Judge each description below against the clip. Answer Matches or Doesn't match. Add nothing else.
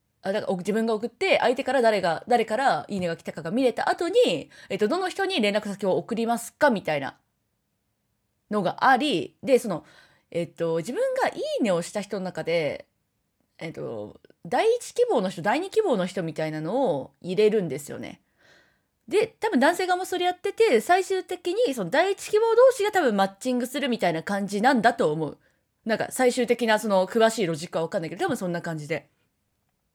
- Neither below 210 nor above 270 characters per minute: Doesn't match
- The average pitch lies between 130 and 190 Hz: Doesn't match